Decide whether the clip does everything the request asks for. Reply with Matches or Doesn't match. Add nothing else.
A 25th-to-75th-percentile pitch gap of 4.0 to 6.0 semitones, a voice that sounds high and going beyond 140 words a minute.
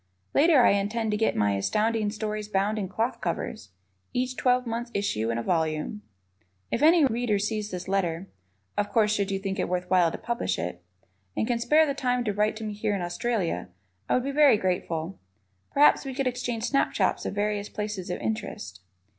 Matches